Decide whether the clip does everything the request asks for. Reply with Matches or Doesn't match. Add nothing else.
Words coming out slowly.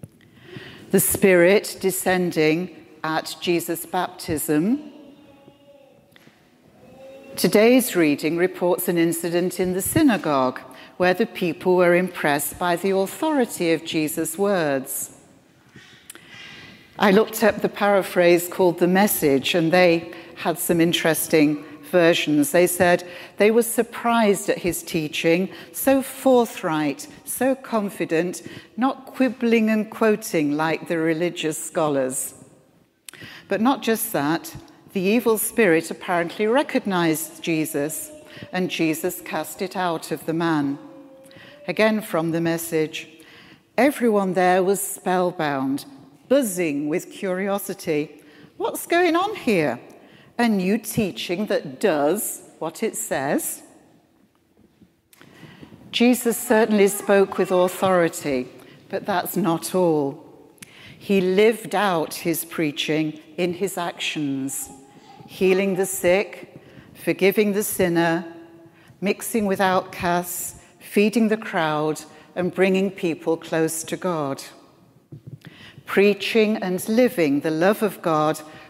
Matches